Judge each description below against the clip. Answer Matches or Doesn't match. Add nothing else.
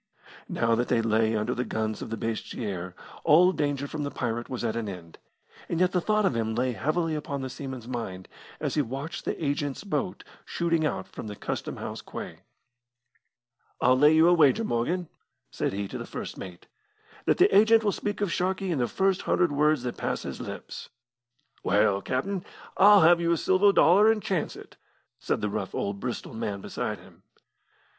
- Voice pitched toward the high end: Doesn't match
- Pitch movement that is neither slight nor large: Doesn't match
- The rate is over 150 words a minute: Matches